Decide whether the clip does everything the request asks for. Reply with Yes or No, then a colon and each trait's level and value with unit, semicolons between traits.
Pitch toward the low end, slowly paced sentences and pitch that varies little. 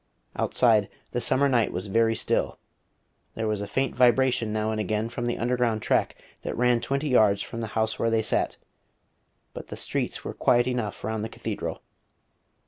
No: low, 115 Hz; average, 180 wpm; narrow, 2.2 semitones